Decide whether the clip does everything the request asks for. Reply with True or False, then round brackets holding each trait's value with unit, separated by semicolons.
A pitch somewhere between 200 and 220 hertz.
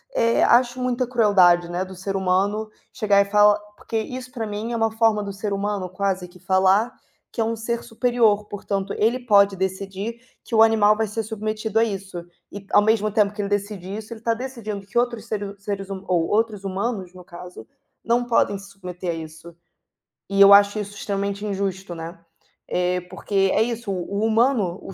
True (205 Hz)